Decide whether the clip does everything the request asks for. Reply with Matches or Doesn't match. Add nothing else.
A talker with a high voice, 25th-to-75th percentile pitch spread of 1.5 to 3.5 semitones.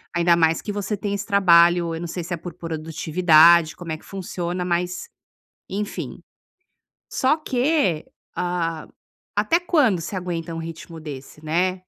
Doesn't match